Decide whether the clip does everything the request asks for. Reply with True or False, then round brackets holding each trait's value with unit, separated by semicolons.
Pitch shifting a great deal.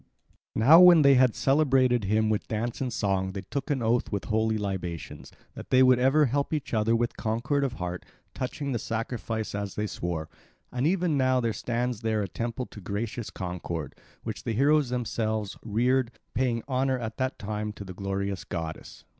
False (4.0 semitones)